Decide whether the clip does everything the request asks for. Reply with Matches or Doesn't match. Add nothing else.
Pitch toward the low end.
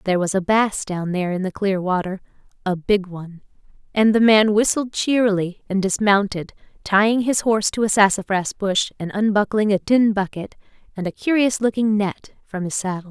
Doesn't match